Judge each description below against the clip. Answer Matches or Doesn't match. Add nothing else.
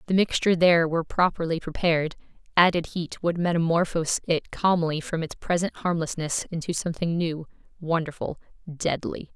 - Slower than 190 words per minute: Matches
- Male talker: Doesn't match